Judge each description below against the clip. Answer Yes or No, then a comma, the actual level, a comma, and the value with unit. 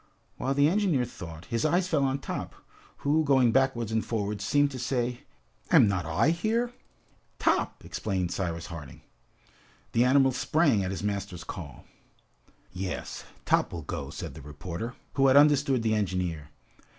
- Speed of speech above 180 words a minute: No, average, 155 wpm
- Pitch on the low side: Yes, low, 115 Hz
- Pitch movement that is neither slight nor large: No, wide, 7.2 semitones